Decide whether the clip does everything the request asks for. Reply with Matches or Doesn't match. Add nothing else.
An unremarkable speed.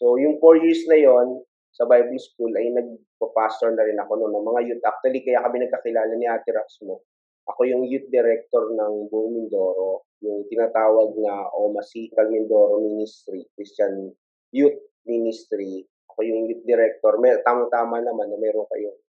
Doesn't match